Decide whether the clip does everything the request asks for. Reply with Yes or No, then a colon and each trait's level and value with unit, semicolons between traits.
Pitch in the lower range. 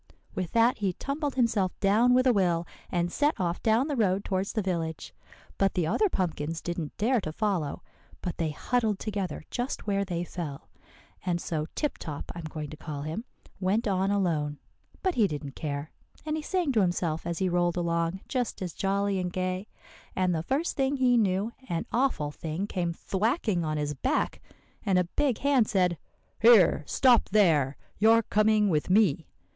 No: high, 190 Hz